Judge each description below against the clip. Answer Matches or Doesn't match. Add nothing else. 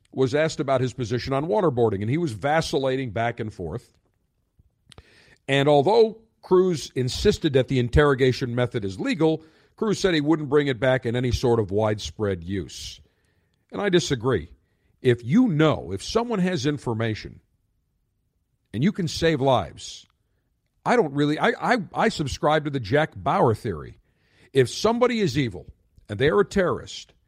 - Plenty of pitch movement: Matches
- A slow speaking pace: Doesn't match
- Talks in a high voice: Doesn't match